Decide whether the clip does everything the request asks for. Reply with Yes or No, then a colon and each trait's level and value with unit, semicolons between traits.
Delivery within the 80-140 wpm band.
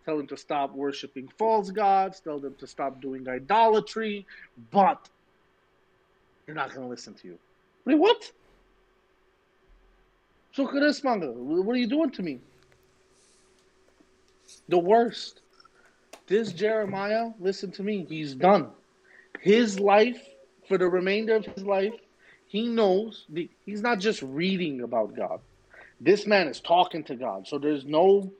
Yes: slow, 135 wpm